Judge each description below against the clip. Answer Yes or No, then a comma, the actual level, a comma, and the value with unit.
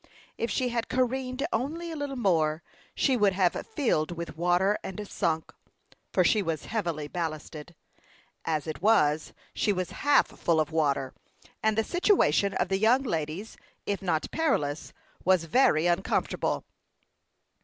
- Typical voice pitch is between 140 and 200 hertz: Yes, high, 190 Hz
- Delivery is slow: No, average, 145 wpm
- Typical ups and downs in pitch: No, wide, 6.9 semitones